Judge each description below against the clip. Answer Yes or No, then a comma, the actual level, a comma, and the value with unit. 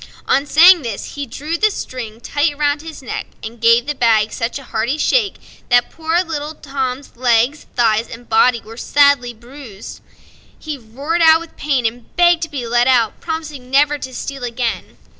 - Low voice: No, very high, 270 Hz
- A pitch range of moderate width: Yes, average, 4.3 semitones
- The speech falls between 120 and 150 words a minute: No, average, 180 wpm